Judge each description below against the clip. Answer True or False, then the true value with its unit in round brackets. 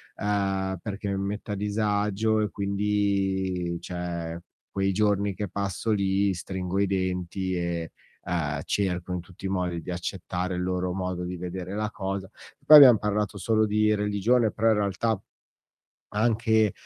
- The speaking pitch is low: True (95 Hz)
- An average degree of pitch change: False (2.3 semitones)